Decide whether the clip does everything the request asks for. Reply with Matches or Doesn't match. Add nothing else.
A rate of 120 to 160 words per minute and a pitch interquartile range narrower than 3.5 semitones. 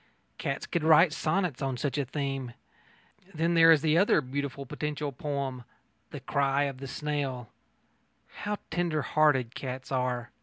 Matches